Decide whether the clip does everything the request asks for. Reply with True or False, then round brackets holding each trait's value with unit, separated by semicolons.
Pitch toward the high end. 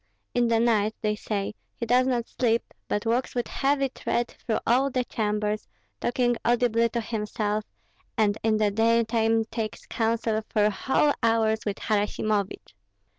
True (225 Hz)